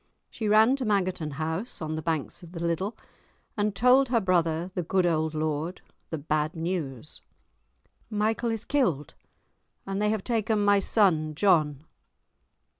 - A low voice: No, medium, 180 Hz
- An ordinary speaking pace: Yes, average, 150 wpm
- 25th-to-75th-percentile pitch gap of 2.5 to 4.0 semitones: No, average, 5.1 semitones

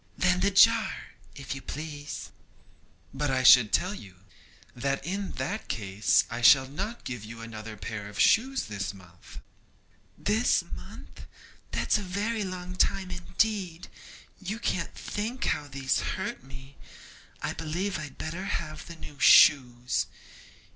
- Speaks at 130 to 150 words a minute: Yes, average, 140 wpm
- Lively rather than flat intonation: Yes, wide, 7.9 semitones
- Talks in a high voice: No, medium, 155 Hz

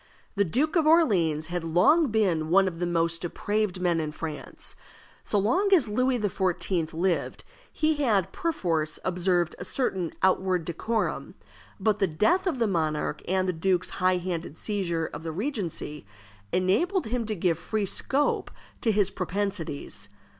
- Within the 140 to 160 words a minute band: Yes, average, 155 wpm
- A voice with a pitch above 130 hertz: Yes, medium, 185 Hz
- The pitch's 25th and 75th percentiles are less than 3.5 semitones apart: No, average, 4.6 semitones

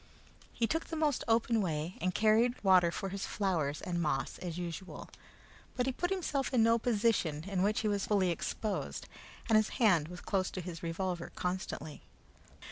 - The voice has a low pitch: No, high, 195 Hz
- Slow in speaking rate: No, average, 175 wpm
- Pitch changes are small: No, average, 4.7 semitones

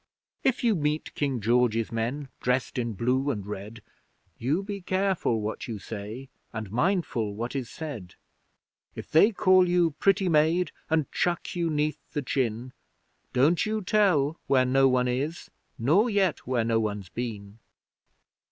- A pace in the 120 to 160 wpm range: Yes, average, 150 wpm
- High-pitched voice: No, low, 135 Hz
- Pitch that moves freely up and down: Yes, wide, 7.0 semitones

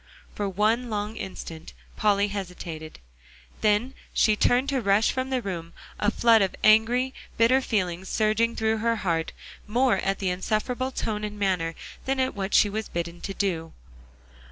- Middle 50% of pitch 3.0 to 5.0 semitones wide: Yes, average, 3.4 semitones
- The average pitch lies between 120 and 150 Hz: No, high, 210 Hz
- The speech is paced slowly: No, average, 160 wpm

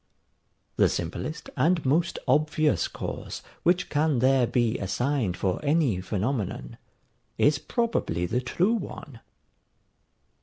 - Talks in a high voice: No, low, 135 Hz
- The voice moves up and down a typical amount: No, wide, 6.2 semitones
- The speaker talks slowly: Yes, slow, 110 wpm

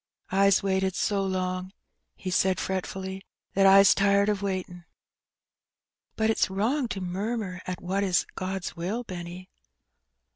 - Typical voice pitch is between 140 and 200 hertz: Yes, high, 190 Hz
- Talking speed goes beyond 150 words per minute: No, slow, 135 wpm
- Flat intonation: Yes, narrow, 1.4 semitones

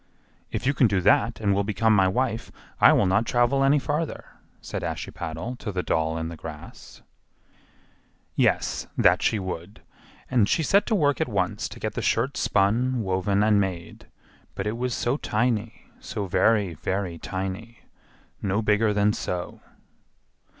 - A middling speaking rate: Yes, average, 160 wpm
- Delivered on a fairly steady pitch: No, average, 4.2 semitones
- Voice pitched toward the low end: Yes, low, 105 Hz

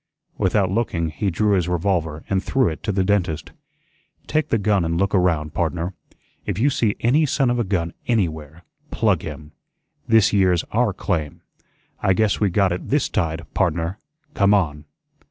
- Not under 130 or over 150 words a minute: No, average, 170 wpm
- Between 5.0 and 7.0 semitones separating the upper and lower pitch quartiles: No, average, 4.1 semitones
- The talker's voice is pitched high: No, very low, 95 Hz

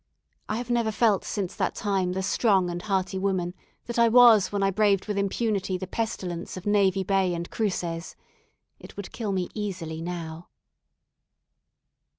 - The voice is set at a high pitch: Yes, high, 195 Hz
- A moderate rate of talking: Yes, average, 165 wpm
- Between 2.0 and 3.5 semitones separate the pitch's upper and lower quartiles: Yes, average, 2.8 semitones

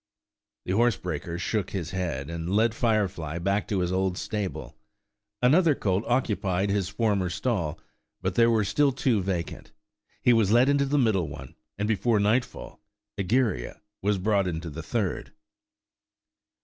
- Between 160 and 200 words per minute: No, average, 150 wpm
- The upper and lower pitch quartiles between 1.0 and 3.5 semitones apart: No, average, 4.2 semitones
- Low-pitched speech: Yes, low, 100 Hz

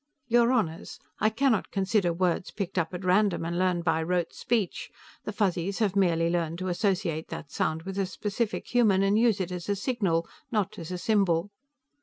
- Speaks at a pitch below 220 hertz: Yes, high, 190 Hz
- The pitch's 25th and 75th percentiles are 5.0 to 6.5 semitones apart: No, average, 3.5 semitones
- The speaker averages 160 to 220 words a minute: Yes, average, 190 wpm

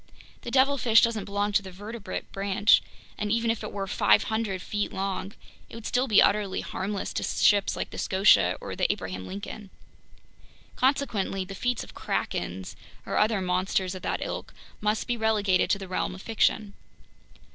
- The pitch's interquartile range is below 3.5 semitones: Yes, narrow, 2.5 semitones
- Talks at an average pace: Yes, average, 170 wpm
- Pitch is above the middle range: Yes, high, 205 Hz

